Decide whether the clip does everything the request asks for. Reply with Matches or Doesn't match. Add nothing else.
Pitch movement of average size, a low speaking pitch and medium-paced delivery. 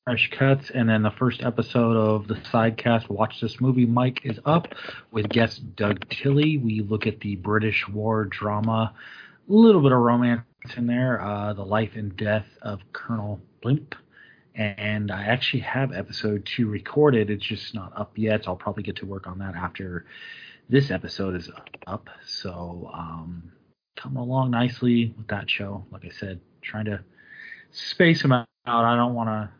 Matches